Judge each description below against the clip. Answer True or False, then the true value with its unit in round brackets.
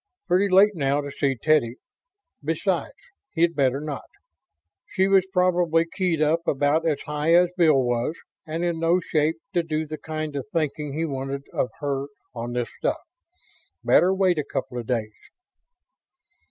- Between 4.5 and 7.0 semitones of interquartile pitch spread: False (3.6 semitones)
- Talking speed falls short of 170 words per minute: True (160 wpm)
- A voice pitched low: False (155 Hz)